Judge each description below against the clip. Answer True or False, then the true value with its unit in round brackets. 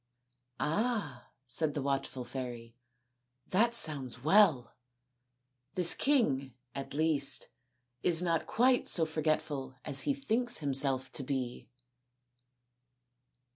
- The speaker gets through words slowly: True (110 wpm)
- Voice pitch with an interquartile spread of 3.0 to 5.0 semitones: False (5.4 semitones)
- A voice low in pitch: False (145 Hz)